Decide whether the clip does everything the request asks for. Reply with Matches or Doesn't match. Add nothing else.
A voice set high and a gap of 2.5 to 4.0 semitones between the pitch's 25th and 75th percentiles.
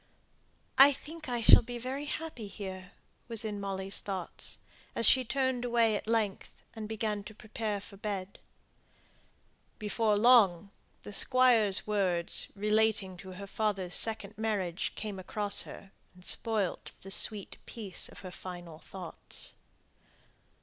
Matches